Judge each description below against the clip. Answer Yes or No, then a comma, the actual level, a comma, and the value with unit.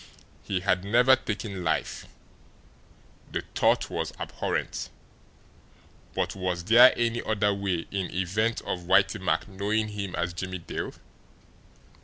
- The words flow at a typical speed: No, slow, 125 wpm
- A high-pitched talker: No, low, 100 Hz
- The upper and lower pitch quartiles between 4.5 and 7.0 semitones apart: No, average, 2.9 semitones